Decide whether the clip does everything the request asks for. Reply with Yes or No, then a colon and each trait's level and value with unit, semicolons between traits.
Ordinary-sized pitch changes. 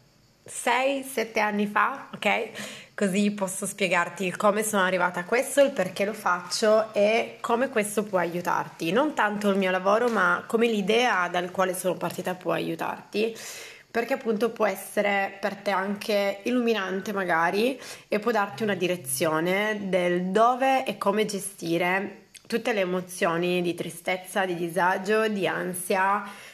Yes: average, 3.1 semitones